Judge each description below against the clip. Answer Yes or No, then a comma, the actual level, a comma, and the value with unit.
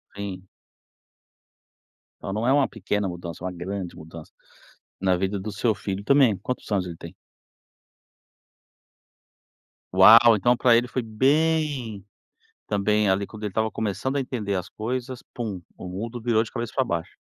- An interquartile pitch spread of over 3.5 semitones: Yes, average, 4.1 semitones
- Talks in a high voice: No, low, 105 Hz